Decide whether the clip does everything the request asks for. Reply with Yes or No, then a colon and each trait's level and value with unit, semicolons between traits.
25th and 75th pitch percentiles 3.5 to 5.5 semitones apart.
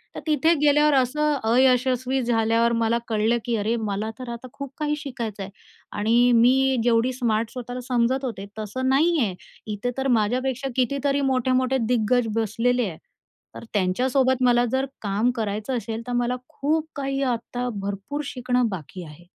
No: average, 2.9 semitones